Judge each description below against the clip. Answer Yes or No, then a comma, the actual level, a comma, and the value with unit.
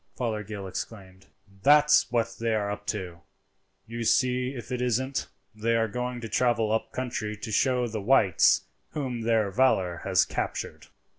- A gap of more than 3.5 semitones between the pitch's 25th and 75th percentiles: No, average, 3.0 semitones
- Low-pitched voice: Yes, low, 115 Hz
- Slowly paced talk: No, average, 155 wpm